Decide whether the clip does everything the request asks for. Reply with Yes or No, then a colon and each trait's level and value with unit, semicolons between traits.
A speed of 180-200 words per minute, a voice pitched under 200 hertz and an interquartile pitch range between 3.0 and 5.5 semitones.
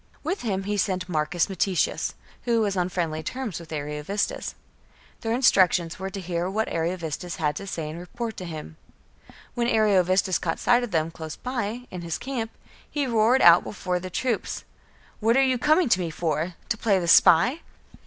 Yes: average, 185 wpm; medium, 185 Hz; average, 5.2 semitones